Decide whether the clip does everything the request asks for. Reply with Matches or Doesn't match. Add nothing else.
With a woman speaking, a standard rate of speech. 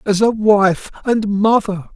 Doesn't match